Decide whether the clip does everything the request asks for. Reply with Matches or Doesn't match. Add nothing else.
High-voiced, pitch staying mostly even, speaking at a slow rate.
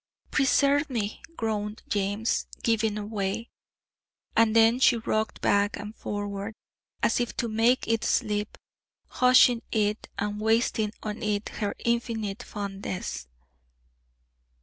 Matches